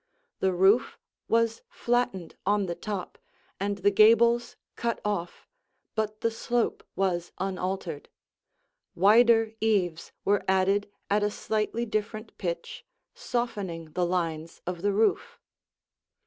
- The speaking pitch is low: No, high, 205 Hz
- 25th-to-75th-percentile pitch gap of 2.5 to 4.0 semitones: Yes, average, 3.4 semitones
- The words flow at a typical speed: No, slow, 120 wpm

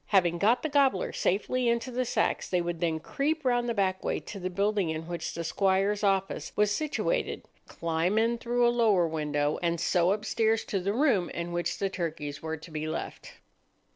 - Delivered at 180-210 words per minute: Yes, average, 200 wpm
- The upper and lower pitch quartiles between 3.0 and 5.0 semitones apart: No, wide, 5.4 semitones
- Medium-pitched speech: No, high, 195 Hz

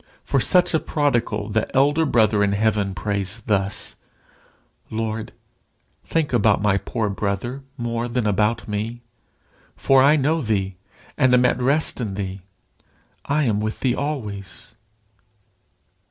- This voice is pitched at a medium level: No, low, 110 Hz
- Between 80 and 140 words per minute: Yes, slow, 135 wpm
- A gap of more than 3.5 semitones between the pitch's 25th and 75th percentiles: Yes, average, 4.3 semitones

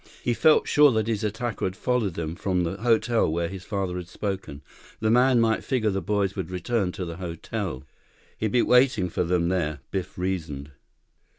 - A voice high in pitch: No, very low, 95 Hz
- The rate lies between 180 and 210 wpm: Yes, average, 190 wpm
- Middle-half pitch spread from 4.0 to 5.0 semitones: Yes, average, 4.3 semitones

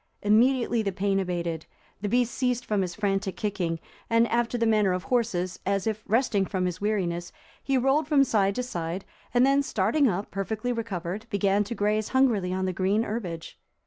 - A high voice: Yes, high, 205 Hz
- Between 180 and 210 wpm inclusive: Yes, average, 185 wpm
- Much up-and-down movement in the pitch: No, average, 4.0 semitones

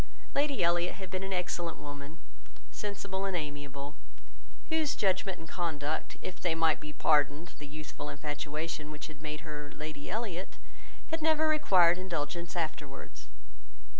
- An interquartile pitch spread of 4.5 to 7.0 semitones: No, average, 4.0 semitones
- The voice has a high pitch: No, medium, 165 Hz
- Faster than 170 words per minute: No, slow, 135 wpm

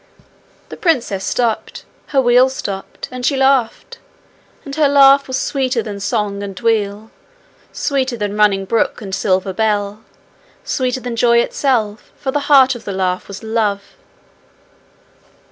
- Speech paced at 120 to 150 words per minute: Yes, average, 145 wpm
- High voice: Yes, high, 230 Hz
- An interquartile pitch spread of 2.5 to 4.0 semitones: No, average, 4.5 semitones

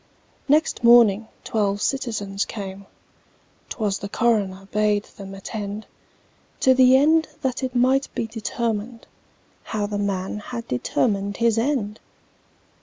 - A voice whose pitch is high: Yes, high, 215 Hz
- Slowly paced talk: Yes, slow, 120 wpm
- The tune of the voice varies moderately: Yes, average, 3.2 semitones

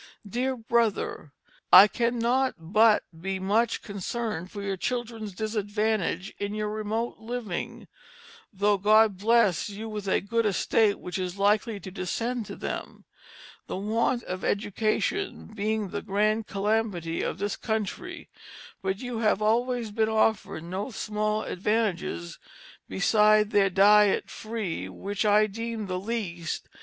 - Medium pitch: No, high, 210 Hz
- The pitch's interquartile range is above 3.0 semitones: No, narrow, 2.4 semitones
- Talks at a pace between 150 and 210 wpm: No, slow, 135 wpm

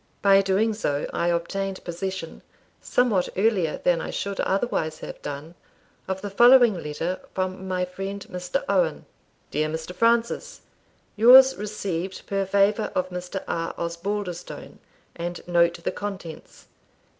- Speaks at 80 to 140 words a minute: Yes, slow, 135 wpm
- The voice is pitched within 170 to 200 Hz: Yes, high, 190 Hz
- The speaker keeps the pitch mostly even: No, average, 3.1 semitones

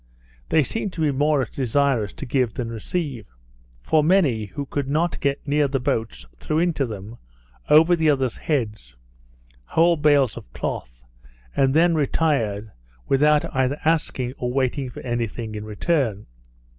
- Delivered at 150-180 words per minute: Yes, average, 155 wpm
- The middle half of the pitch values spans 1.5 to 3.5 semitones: No, average, 4.9 semitones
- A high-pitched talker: No, low, 135 Hz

